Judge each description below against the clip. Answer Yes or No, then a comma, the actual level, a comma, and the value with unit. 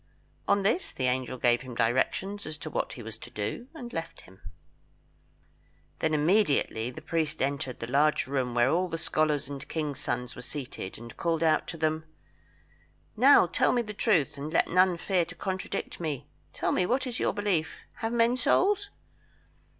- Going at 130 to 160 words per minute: No, average, 185 wpm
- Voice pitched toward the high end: No, medium, 155 Hz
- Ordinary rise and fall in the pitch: No, wide, 6.4 semitones